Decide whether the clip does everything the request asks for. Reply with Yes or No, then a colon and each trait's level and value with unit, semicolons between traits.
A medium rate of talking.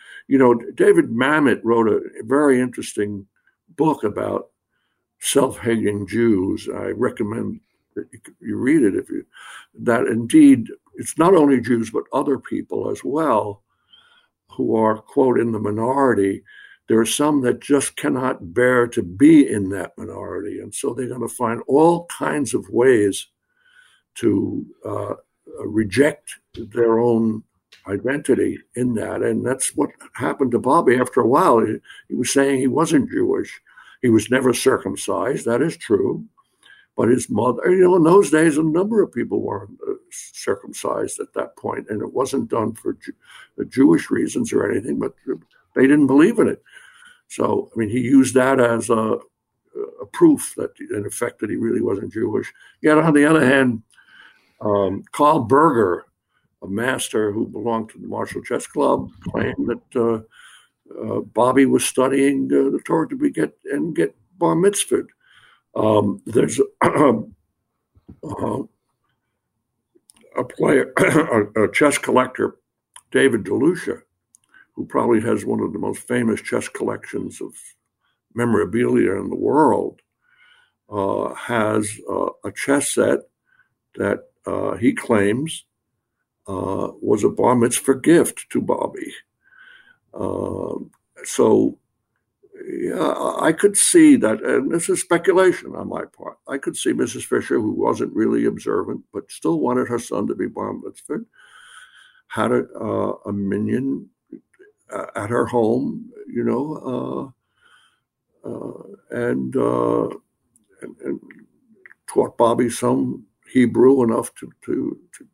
Yes: average, 145 wpm